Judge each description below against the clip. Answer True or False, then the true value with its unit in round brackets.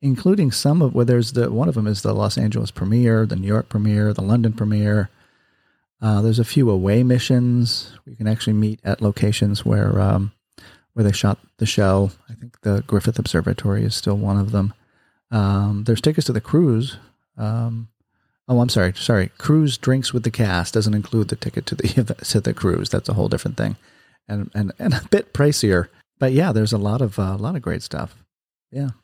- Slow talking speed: False (205 wpm)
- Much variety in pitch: False (2.9 semitones)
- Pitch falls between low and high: False (110 Hz)